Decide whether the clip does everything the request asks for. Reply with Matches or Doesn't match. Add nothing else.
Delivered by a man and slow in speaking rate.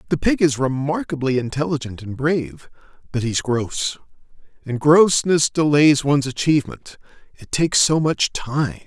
Matches